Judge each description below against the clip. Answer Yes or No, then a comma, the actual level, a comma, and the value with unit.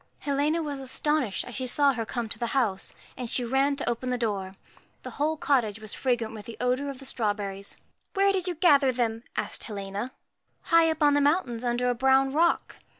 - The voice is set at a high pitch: Yes, very high, 255 Hz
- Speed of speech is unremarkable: No, fast, 215 wpm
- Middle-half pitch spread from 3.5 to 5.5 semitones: Yes, average, 4.1 semitones